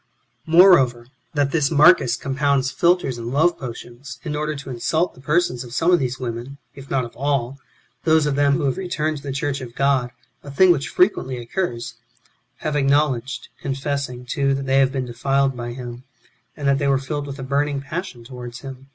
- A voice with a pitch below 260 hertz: Yes, low, 135 Hz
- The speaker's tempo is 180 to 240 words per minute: Yes, fast, 205 wpm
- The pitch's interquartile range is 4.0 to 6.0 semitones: No, average, 2.7 semitones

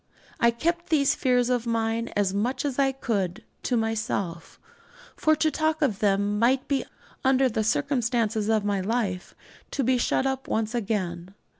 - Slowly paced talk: No, average, 170 wpm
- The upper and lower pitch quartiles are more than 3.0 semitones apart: Yes, average, 4.4 semitones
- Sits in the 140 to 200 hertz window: No, high, 230 Hz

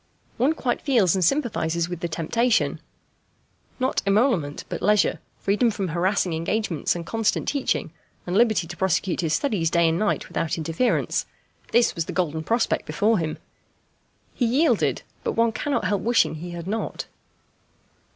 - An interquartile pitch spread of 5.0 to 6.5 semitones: Yes, wide, 5.6 semitones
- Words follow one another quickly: No, average, 155 wpm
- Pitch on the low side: No, high, 195 Hz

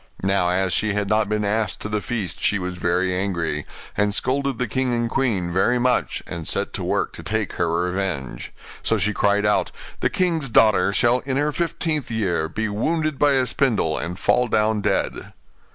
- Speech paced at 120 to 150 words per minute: No, average, 195 wpm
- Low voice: Yes, low, 105 Hz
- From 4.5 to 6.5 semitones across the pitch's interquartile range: Yes, average, 5.1 semitones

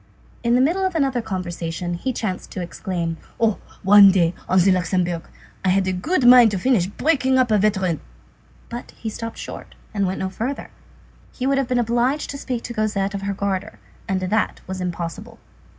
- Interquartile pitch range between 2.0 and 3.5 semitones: No, average, 4.7 semitones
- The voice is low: No, high, 205 Hz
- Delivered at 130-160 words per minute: No, average, 195 wpm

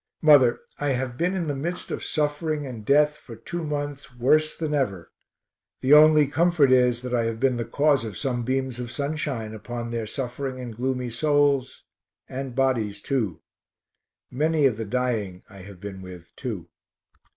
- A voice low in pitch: Yes, low, 130 Hz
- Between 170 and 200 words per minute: Yes, average, 175 wpm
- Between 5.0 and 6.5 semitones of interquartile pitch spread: No, average, 3.9 semitones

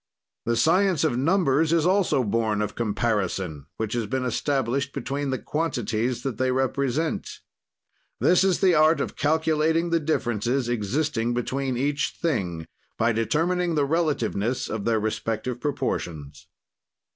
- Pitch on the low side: Yes, low, 130 Hz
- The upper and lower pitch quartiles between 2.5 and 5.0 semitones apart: No, wide, 5.6 semitones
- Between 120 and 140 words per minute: Yes, slow, 135 wpm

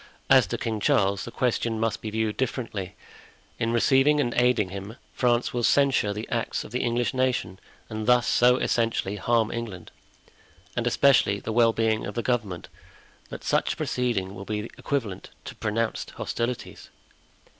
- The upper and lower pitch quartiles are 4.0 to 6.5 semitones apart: No, average, 2.7 semitones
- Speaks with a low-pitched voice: Yes, low, 115 Hz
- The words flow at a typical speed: Yes, average, 165 wpm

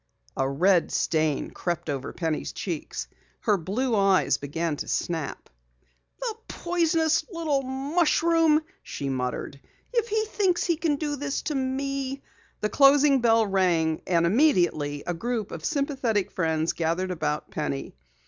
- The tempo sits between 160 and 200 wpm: No, average, 140 wpm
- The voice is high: Yes, high, 215 Hz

